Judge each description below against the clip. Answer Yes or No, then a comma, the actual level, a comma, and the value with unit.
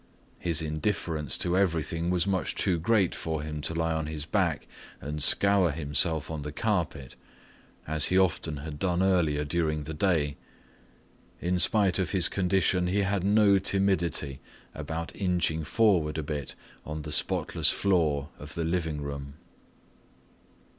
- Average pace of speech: Yes, average, 150 wpm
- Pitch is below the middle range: Yes, very low, 80 Hz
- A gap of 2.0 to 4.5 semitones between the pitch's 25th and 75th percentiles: Yes, average, 3.5 semitones